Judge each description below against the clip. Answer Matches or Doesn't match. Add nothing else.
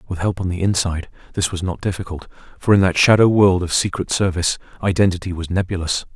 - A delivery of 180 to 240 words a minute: Matches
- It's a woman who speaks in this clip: Doesn't match